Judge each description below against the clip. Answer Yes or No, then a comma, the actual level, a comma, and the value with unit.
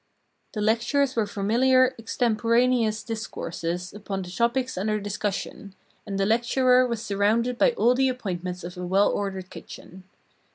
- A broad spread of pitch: No, average, 4.0 semitones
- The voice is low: No, high, 215 Hz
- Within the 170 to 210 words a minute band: No, average, 140 wpm